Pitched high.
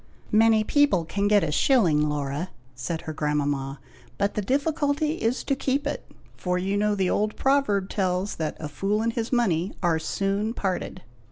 Yes: high, 200 Hz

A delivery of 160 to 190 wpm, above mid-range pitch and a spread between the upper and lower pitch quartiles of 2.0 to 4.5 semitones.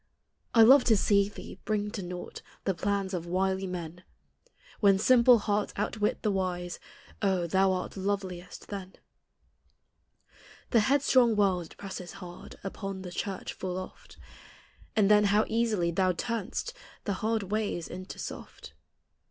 No: average, 145 wpm; high, 195 Hz; narrow, 2.5 semitones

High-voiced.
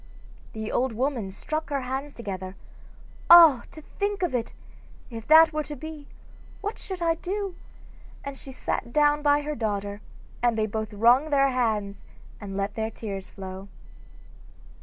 Yes: very high, 255 Hz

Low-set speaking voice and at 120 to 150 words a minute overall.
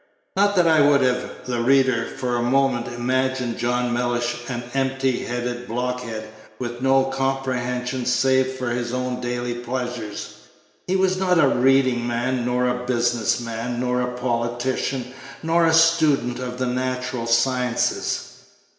Yes: low, 125 Hz; average, 145 wpm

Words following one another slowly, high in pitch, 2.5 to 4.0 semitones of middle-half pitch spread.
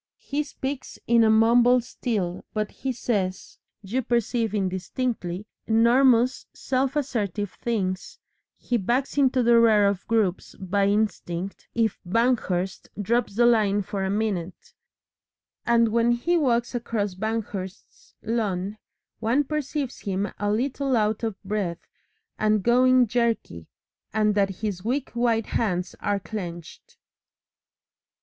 Yes: slow, 125 wpm; high, 220 Hz; average, 3.5 semitones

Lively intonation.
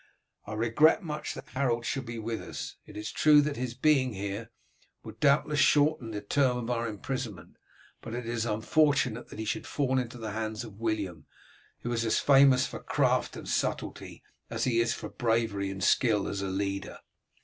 No: average, 3.7 semitones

